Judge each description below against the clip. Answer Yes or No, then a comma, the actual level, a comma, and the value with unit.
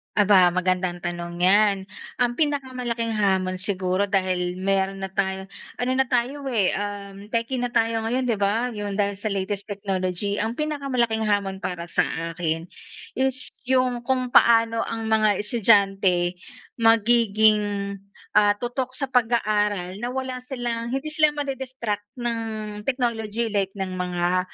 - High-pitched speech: Yes, high, 210 Hz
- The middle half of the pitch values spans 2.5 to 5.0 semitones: Yes, average, 4.0 semitones